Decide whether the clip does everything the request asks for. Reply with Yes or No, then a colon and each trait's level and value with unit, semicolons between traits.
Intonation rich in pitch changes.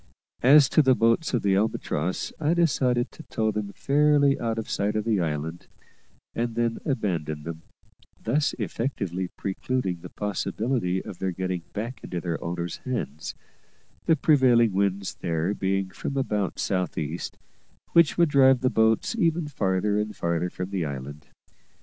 Yes: wide, 6.2 semitones